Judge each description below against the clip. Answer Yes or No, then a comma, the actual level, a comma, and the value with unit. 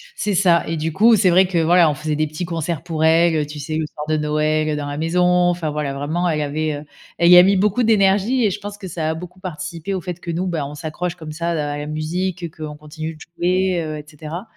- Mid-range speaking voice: Yes, medium, 165 Hz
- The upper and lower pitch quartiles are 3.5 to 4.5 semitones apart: No, average, 2.8 semitones